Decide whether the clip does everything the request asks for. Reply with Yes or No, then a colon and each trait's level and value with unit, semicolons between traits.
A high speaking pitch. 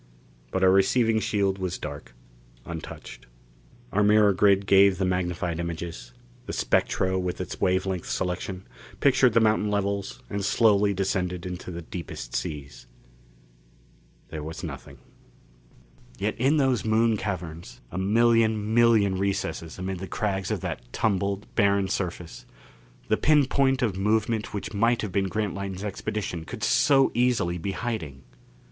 No: low, 100 Hz